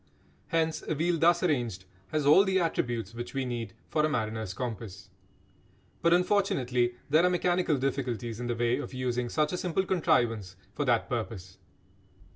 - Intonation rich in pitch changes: Yes, wide, 5.9 semitones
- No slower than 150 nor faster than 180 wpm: Yes, average, 165 wpm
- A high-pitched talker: No, low, 125 Hz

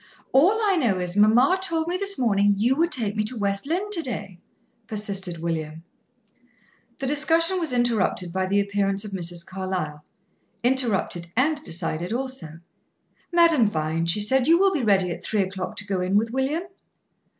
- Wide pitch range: Yes, wide, 7.1 semitones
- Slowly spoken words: No, average, 175 wpm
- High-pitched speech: Yes, high, 210 Hz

